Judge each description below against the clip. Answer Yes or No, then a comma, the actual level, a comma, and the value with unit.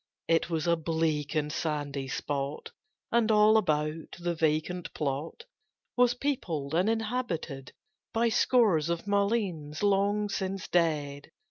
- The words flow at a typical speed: No, slow, 125 wpm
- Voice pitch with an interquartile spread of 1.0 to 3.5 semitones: No, wide, 5.6 semitones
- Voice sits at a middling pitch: Yes, medium, 170 Hz